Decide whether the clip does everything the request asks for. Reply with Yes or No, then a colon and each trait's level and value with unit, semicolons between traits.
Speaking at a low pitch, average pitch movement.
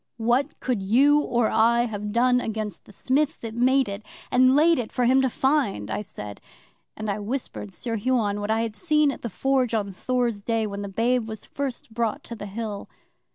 No: high, 230 Hz; average, 3.6 semitones